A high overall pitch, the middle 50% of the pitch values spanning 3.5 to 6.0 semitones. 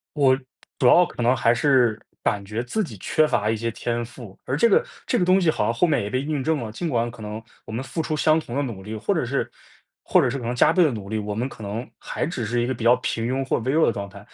No: low, 120 Hz; average, 4.4 semitones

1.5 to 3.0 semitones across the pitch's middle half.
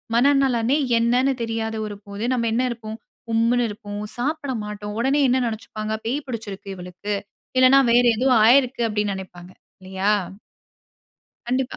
No: average, 3.6 semitones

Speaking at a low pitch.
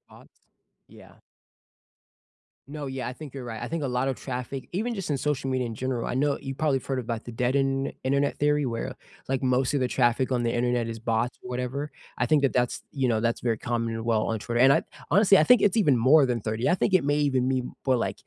Yes: low, 130 Hz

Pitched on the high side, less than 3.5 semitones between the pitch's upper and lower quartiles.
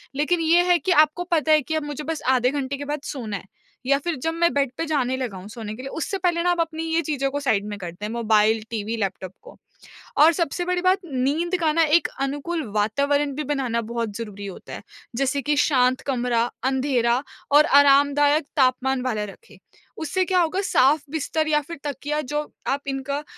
No: very high, 280 Hz; average, 4.3 semitones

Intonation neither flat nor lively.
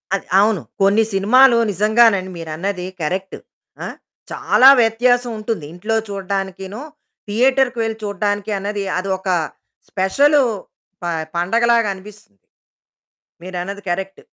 Yes: average, 3.0 semitones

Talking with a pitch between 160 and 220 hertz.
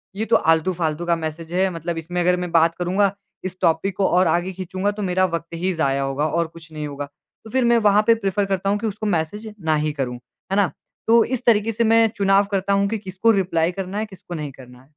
Yes: medium, 185 Hz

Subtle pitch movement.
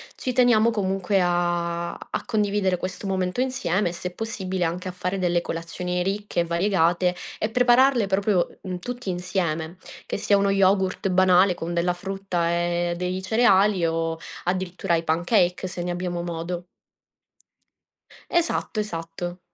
Yes: narrow, 2.3 semitones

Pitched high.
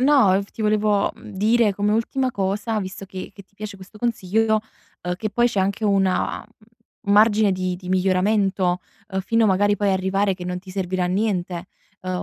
Yes: high, 200 Hz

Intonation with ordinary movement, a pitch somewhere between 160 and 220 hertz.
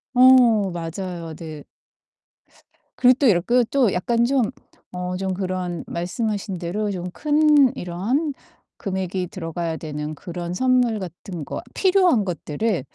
No: wide, 5.8 semitones; high, 190 Hz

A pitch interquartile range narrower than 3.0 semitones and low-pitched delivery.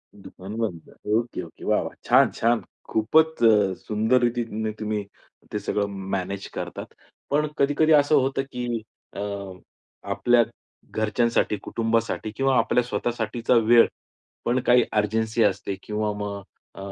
Yes: narrow, 2.6 semitones; low, 115 Hz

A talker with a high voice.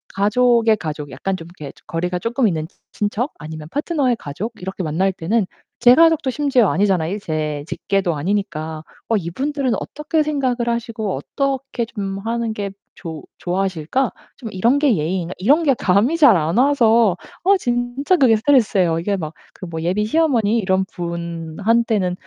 Yes: high, 205 Hz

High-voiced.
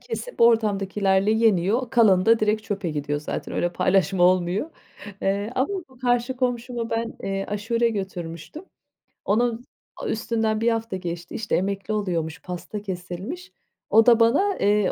Yes: high, 210 Hz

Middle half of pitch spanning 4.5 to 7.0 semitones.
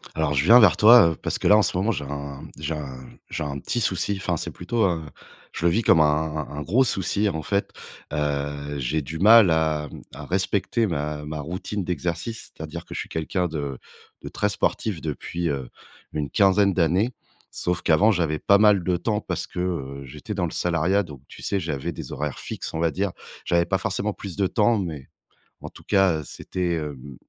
Yes: average, 4.8 semitones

